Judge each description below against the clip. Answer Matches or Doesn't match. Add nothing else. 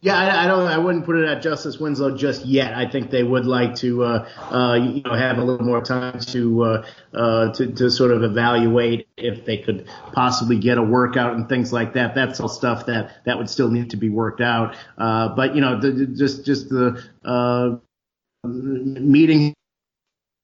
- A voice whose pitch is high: Doesn't match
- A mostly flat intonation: Matches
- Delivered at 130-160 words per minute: Doesn't match